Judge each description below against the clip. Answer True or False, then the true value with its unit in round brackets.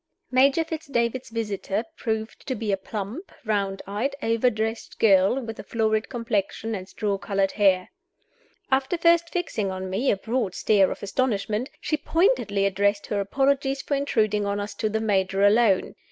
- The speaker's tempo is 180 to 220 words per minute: False (165 wpm)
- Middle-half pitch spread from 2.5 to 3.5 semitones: False (4.5 semitones)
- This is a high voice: True (220 Hz)